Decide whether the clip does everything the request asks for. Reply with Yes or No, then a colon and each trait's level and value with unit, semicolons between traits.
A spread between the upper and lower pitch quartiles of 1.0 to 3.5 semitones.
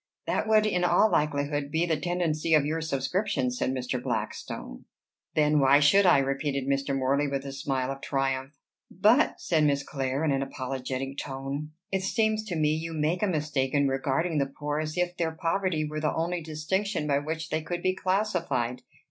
No: average, 4.0 semitones